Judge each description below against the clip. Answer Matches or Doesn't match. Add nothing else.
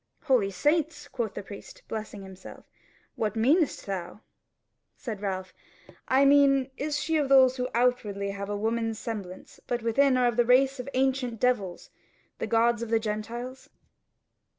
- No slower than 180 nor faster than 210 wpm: Doesn't match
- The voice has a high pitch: Matches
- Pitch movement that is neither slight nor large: Matches